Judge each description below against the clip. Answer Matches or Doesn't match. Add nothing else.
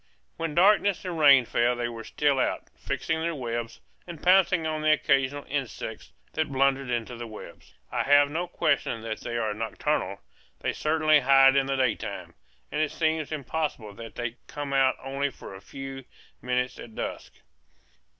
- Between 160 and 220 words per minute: Matches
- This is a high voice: Doesn't match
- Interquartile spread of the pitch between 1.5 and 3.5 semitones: Doesn't match